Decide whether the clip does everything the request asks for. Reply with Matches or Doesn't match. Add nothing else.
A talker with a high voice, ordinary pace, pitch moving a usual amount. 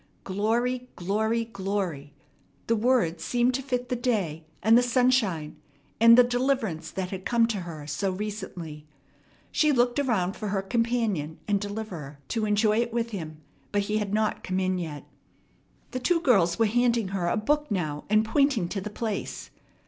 Matches